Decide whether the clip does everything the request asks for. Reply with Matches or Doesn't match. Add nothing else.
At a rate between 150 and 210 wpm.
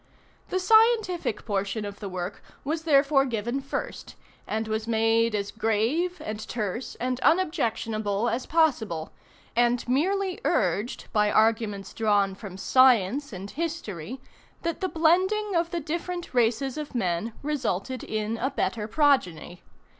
Doesn't match